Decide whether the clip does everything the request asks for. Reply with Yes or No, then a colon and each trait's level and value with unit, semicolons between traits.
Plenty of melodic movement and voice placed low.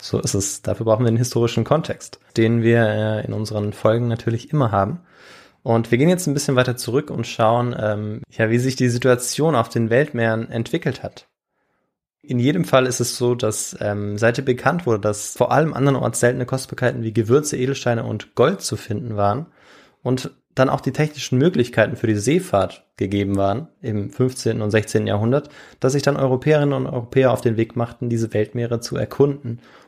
No: average, 3.0 semitones; low, 120 Hz